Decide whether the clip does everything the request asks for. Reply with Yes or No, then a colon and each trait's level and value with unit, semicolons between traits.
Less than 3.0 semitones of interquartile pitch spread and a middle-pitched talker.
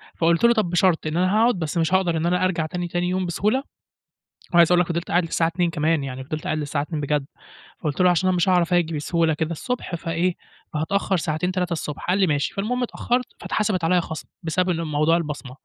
Yes: narrow, 2.6 semitones; medium, 170 Hz